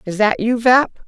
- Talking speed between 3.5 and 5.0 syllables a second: Yes, 4.9 syllables/s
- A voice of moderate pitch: No, high, 225 Hz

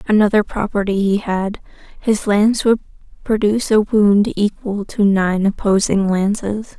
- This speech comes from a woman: Yes, female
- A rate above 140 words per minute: No, slow, 135 wpm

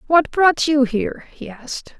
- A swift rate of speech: No, average, 180 wpm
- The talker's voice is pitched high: Yes, very high, 275 Hz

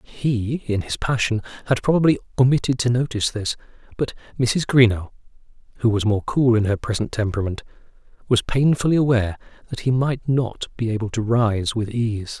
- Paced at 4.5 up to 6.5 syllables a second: Yes, 5.5 syllables/s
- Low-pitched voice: Yes, low, 115 Hz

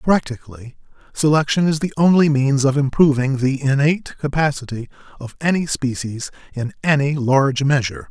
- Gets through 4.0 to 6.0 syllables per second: Yes, 5.3 syllables/s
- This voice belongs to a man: Yes, male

